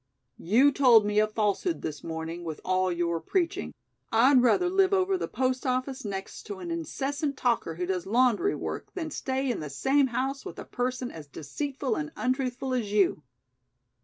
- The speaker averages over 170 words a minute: Yes, average, 180 wpm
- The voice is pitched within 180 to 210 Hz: No, high, 245 Hz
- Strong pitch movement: Yes, wide, 6.6 semitones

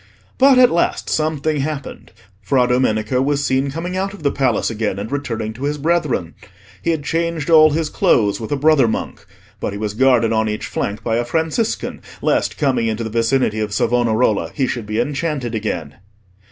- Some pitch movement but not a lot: No, wide, 5.7 semitones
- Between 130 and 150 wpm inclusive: No, average, 190 wpm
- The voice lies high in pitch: No, low, 130 Hz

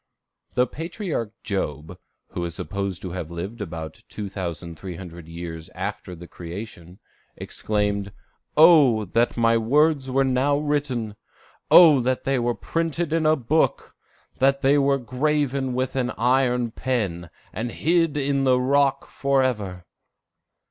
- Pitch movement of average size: No, wide, 6.7 semitones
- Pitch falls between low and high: No, low, 120 Hz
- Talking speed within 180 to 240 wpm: No, slow, 135 wpm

